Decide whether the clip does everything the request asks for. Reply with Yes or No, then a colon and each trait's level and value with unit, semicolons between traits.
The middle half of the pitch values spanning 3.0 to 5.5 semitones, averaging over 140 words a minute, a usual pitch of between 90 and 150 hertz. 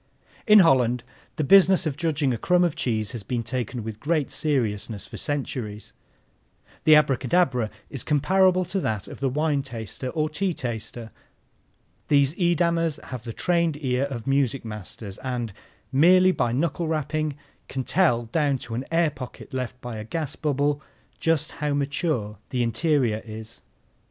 Yes: average, 5.1 semitones; average, 155 wpm; medium, 140 Hz